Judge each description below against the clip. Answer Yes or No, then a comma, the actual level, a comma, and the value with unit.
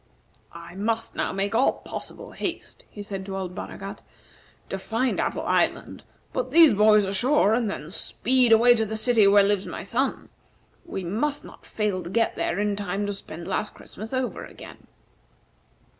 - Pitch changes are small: No, average, 3.1 semitones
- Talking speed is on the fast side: No, average, 175 wpm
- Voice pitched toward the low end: No, high, 210 Hz